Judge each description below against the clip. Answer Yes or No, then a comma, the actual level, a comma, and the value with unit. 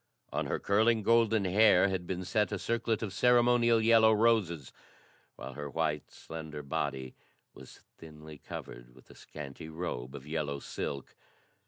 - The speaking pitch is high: No, very low, 90 Hz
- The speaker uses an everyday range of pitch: No, wide, 7.0 semitones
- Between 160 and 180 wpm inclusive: No, average, 150 wpm